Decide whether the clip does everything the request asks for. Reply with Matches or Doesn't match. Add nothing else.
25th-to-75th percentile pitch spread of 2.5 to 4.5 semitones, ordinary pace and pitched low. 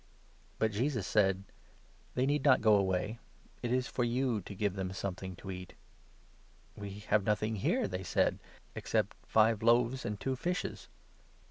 Matches